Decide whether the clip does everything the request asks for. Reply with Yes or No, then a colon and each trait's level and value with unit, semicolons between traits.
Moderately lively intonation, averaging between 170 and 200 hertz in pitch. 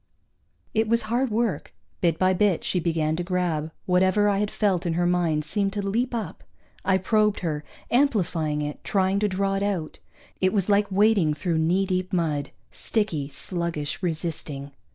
Yes: average, 4.0 semitones; medium, 185 Hz